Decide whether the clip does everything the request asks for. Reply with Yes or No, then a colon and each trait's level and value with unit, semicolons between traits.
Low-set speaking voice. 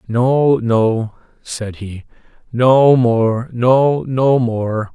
Yes: low, 120 Hz